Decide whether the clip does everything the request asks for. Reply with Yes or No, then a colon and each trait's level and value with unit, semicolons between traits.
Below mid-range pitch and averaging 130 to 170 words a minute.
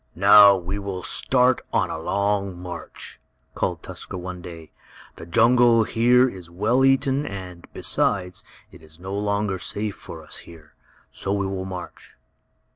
Yes: low, 100 Hz; average, 150 wpm